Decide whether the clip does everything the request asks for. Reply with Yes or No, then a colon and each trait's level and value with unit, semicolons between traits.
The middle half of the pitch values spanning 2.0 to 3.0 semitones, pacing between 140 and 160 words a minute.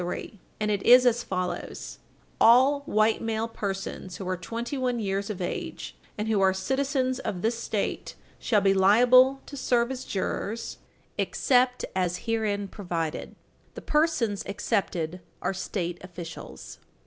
No: average, 4.5 semitones; average, 145 wpm